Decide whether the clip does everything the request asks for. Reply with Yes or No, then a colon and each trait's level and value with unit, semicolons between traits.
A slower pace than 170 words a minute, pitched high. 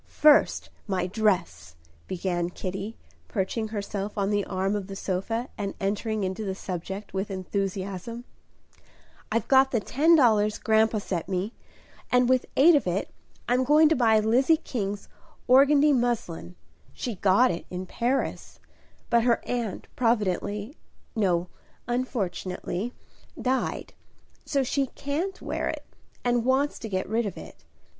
Yes: average, 140 wpm; high, 215 Hz